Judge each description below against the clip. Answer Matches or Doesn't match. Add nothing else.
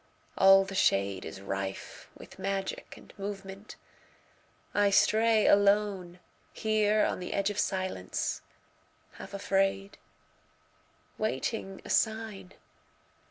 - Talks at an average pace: Doesn't match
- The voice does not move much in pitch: Matches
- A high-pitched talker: Matches